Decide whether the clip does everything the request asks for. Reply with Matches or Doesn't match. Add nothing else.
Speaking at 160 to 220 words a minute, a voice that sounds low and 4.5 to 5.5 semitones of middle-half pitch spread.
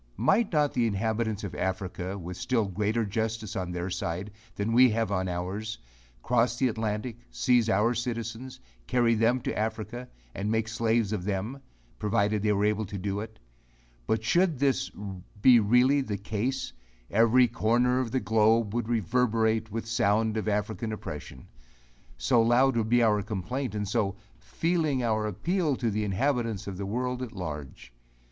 Doesn't match